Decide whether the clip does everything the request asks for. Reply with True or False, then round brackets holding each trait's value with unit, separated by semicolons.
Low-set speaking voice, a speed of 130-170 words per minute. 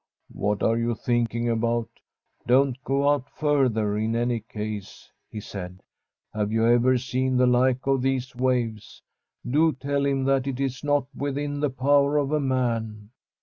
True (125 Hz; 165 wpm)